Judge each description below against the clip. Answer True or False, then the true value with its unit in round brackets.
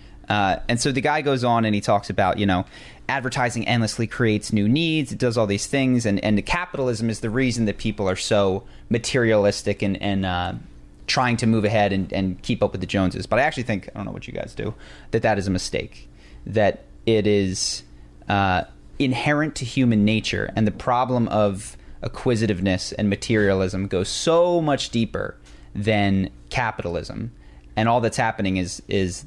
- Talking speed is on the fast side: False (195 wpm)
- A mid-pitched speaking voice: False (105 Hz)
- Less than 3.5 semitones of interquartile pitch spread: False (4.1 semitones)